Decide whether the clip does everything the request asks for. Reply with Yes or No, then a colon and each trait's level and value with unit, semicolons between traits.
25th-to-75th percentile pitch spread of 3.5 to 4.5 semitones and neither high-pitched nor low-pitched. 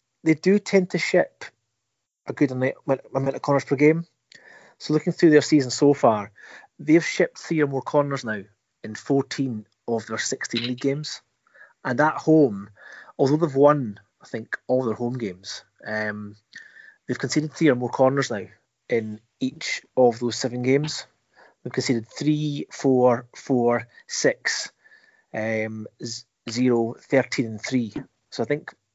No: average, 4.1 semitones; low, 130 Hz